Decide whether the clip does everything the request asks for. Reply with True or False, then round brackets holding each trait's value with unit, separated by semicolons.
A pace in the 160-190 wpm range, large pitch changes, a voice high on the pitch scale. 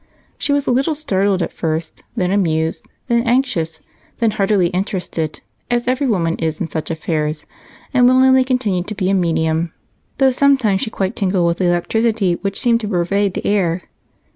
True (175 wpm; 5.8 semitones; 195 Hz)